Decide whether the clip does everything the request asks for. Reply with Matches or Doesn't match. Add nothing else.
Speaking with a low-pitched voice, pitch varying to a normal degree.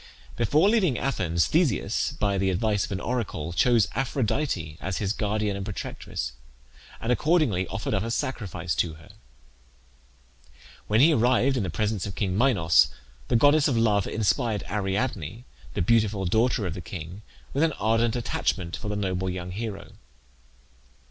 Matches